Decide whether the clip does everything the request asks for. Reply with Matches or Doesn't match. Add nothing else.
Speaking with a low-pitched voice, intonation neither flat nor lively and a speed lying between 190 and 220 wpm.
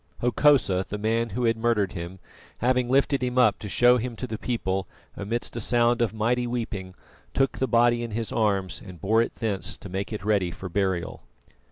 Matches